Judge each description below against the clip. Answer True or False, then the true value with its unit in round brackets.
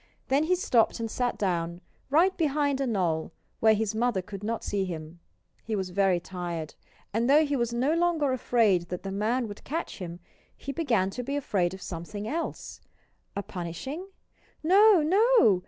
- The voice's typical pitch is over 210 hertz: True (225 Hz)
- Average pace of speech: True (175 wpm)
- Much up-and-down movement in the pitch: True (7.4 semitones)